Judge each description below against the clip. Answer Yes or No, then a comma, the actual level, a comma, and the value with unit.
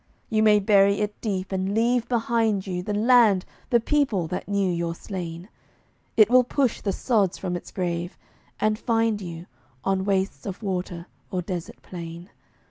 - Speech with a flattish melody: No, average, 3.6 semitones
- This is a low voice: No, high, 195 Hz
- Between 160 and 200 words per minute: Yes, average, 165 wpm